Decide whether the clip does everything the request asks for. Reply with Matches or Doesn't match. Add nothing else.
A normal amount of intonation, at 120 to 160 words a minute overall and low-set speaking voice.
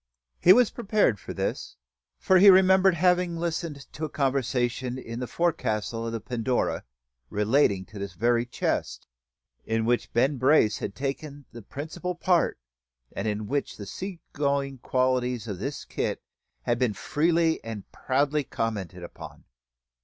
Doesn't match